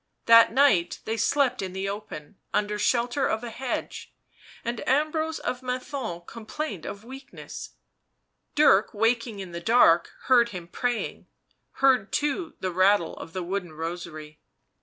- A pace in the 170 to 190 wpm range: No, average, 140 wpm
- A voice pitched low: No, high, 220 Hz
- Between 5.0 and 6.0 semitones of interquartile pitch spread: Yes, wide, 5.6 semitones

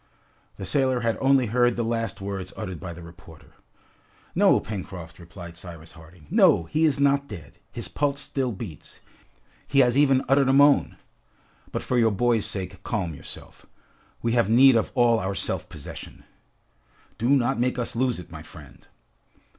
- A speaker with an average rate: Yes, average, 170 wpm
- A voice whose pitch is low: Yes, low, 115 Hz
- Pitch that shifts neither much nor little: No, wide, 6.5 semitones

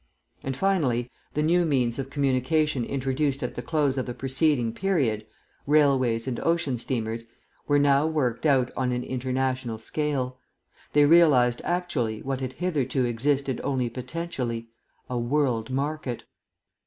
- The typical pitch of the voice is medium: No, low, 130 Hz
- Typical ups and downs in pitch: Yes, average, 3.3 semitones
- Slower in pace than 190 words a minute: Yes, average, 140 wpm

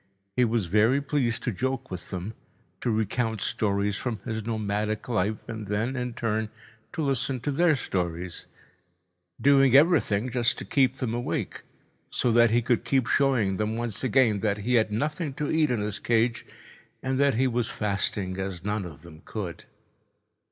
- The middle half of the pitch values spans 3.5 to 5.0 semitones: Yes, average, 4.1 semitones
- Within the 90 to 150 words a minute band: No, average, 165 wpm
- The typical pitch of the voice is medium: No, low, 115 Hz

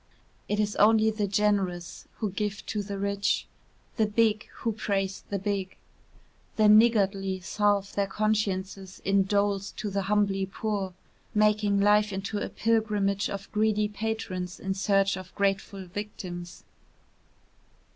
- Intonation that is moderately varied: No, narrow, 1.5 semitones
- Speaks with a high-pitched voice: Yes, high, 200 Hz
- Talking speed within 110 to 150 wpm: Yes, slow, 135 wpm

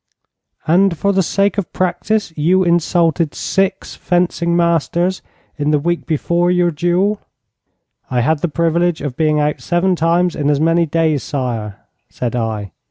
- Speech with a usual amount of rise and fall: Yes, average, 3.0 semitones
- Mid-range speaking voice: Yes, medium, 170 Hz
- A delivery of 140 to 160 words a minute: Yes, average, 155 wpm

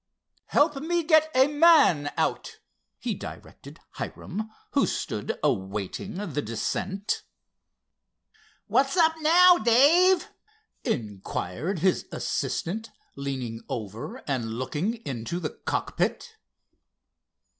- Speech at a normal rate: No, slow, 95 wpm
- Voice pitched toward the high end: Yes, high, 195 Hz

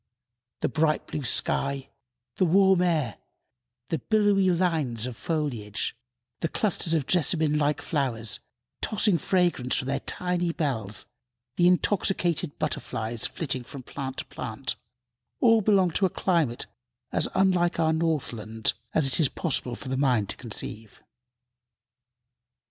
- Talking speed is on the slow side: Yes, slow, 130 wpm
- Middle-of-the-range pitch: Yes, medium, 155 Hz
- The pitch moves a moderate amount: No, wide, 5.8 semitones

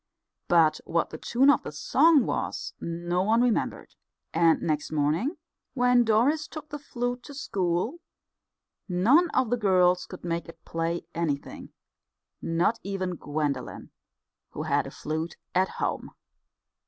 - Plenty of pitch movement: Yes, wide, 6.7 semitones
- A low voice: No, medium, 185 Hz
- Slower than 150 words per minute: Yes, average, 140 wpm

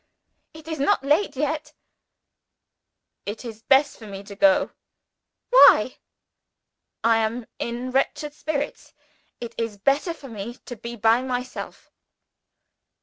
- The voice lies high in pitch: Yes, very high, 255 Hz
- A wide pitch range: No, average, 4.5 semitones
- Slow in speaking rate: Yes, slow, 125 wpm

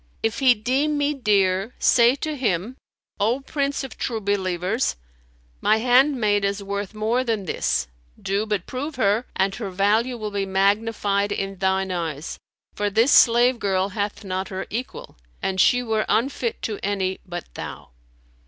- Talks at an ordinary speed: Yes, average, 160 wpm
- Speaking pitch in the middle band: No, high, 210 Hz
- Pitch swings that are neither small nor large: Yes, average, 3.9 semitones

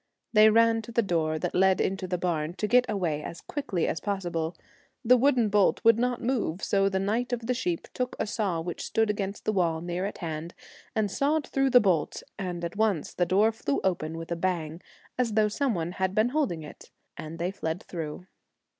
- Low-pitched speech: No, high, 195 Hz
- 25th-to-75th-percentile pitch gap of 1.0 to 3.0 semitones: No, average, 4.8 semitones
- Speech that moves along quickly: Yes, fast, 215 wpm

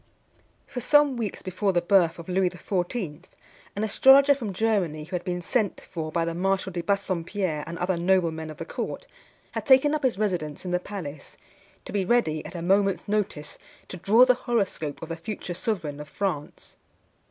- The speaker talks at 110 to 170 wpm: No, average, 185 wpm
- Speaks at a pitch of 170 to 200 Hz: Yes, medium, 185 Hz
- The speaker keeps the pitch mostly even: No, average, 3.9 semitones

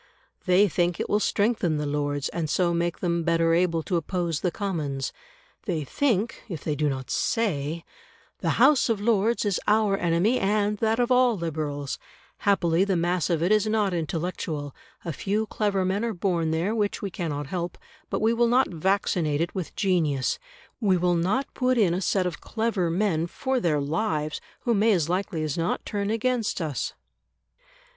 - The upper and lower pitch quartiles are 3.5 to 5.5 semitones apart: Yes, average, 4.4 semitones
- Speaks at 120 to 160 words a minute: No, average, 180 wpm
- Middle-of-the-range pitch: Yes, medium, 180 Hz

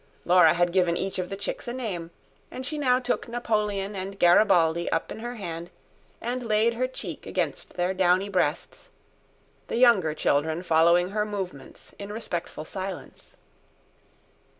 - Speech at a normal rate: Yes, average, 150 wpm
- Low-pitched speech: No, high, 190 Hz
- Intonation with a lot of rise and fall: No, average, 4.5 semitones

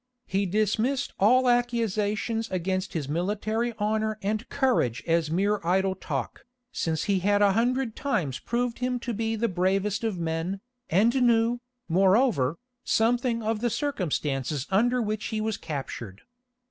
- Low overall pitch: No, high, 210 Hz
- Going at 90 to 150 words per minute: Yes, average, 145 wpm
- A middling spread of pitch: Yes, average, 4.2 semitones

